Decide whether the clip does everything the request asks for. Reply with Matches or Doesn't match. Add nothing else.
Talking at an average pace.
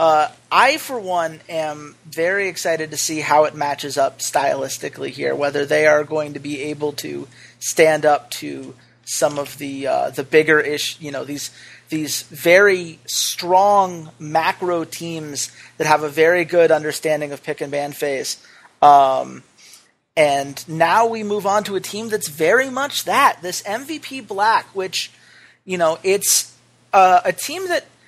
Matches